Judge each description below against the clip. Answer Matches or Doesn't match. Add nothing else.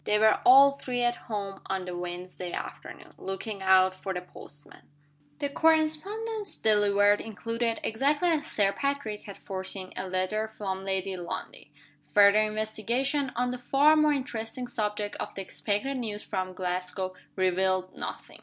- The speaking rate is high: Doesn't match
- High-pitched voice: Matches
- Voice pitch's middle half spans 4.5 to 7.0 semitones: Matches